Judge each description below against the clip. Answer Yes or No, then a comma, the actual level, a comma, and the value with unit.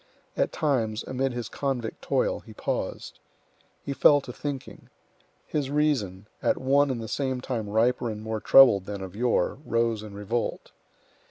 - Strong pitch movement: No, average, 3.8 semitones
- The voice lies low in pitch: Yes, low, 120 Hz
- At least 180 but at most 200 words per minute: No, average, 160 wpm